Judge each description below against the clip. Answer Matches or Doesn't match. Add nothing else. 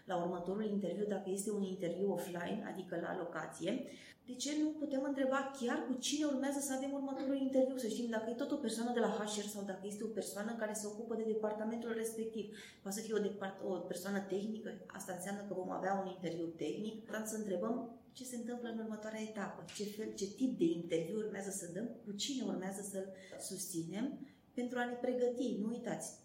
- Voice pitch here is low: Doesn't match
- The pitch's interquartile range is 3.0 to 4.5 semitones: Matches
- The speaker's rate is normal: Doesn't match